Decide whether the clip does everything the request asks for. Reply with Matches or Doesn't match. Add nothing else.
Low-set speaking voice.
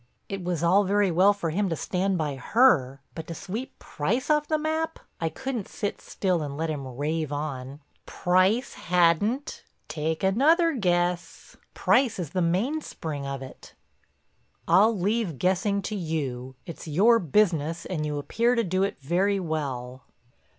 Doesn't match